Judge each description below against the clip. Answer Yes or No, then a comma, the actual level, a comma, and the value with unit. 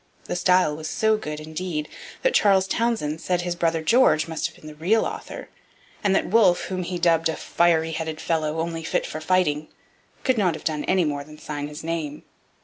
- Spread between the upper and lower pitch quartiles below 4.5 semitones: Yes, average, 3.0 semitones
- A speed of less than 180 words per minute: No, fast, 205 wpm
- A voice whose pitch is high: No, medium, 165 Hz